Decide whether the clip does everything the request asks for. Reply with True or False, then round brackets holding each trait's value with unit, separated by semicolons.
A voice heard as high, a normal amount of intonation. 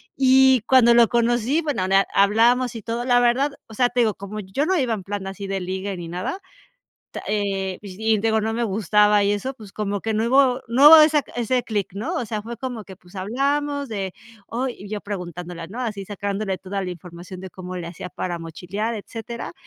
True (215 Hz; 4.0 semitones)